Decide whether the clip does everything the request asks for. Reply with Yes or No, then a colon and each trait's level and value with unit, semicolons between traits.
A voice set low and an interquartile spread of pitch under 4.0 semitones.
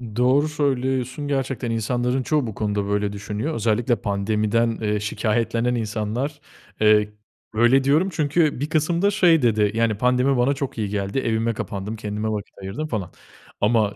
No: low, 115 Hz; average, 4.3 semitones